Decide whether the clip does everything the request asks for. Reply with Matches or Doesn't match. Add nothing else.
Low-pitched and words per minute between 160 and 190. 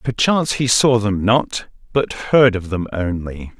Matches